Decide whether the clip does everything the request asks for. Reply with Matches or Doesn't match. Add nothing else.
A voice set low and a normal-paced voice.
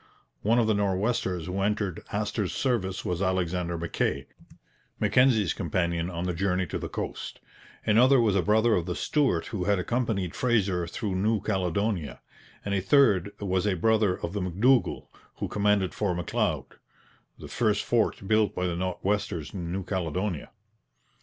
Matches